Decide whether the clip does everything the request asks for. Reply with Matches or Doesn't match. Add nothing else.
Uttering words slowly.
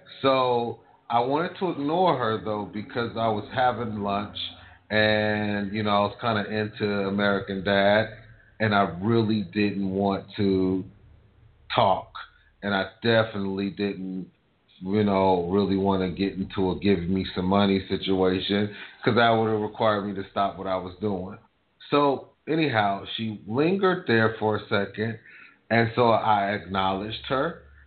Doesn't match